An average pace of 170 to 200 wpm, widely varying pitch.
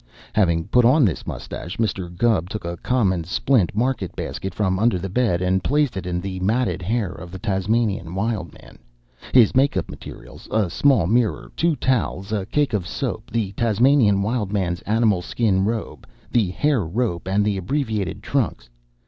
No: average, 175 wpm; average, 4.3 semitones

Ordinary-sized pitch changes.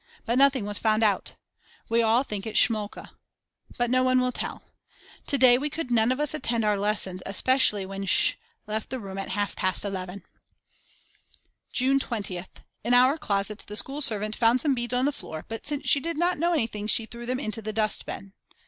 Yes: average, 3.8 semitones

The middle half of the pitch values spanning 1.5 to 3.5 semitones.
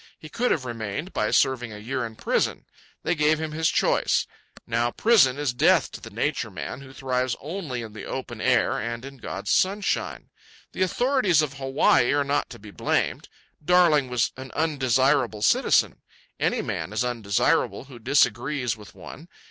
No: average, 4.4 semitones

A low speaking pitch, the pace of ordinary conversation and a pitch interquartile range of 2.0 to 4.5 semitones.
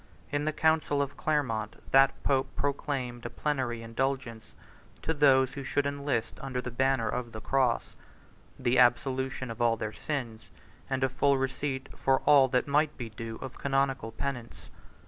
Yes: low, 130 Hz; average, 165 wpm; average, 2.7 semitones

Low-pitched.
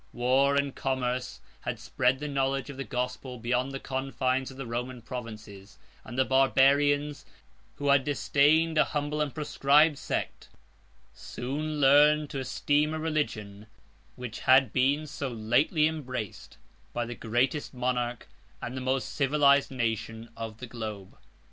Yes: low, 130 Hz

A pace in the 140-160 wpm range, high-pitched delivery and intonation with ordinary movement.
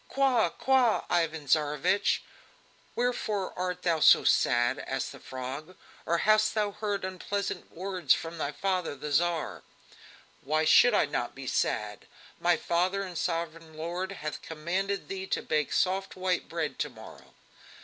No: average, 150 wpm; medium, 175 Hz; average, 4.2 semitones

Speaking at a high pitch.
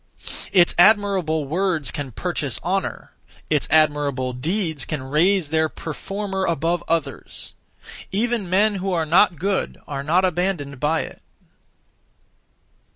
No: medium, 165 Hz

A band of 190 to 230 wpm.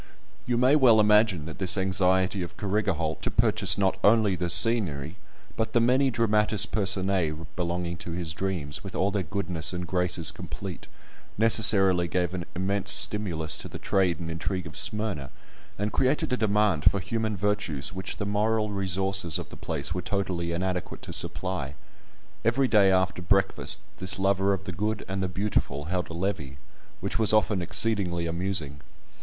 No: average, 170 wpm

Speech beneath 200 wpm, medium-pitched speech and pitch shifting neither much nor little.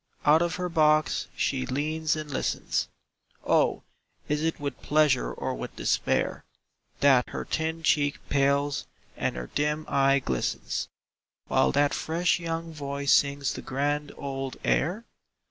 No: average, 140 wpm; medium, 145 Hz; narrow, 2.3 semitones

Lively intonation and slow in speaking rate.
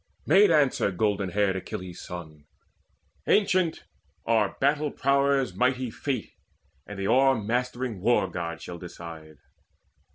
Yes: wide, 7.0 semitones; slow, 110 wpm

